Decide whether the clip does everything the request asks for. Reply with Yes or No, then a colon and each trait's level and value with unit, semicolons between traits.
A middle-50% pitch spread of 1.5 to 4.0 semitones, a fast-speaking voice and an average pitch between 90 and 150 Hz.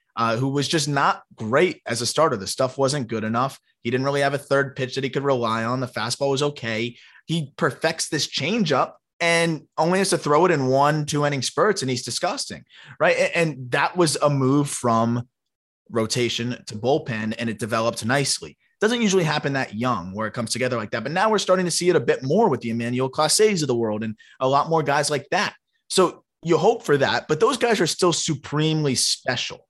No: average, 4.8 semitones; fast, 220 wpm; low, 135 Hz